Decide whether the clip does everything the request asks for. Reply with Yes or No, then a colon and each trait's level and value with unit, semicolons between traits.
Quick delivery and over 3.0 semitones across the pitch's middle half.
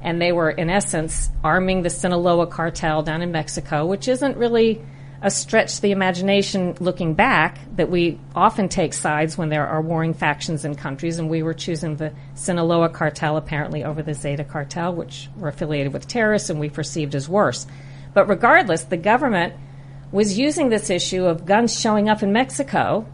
No: average, 180 wpm; average, 4.3 semitones